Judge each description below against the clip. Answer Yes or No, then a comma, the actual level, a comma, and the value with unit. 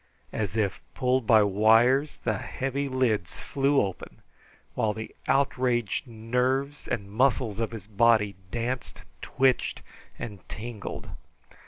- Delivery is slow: Yes, slow, 120 wpm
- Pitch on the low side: Yes, low, 115 Hz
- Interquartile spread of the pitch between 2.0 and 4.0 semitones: Yes, average, 3.5 semitones